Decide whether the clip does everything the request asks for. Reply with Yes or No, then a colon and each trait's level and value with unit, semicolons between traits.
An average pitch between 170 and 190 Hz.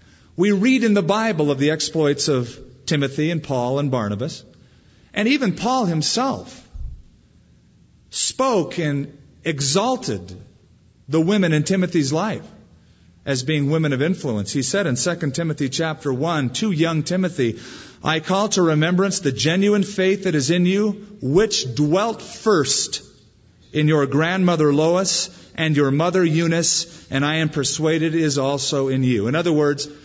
No: medium, 155 Hz